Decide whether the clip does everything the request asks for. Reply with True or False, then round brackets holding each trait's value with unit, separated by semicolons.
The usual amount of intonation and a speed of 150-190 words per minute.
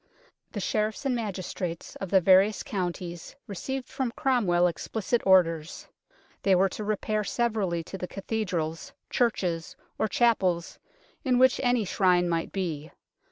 False (4.2 semitones; 135 wpm)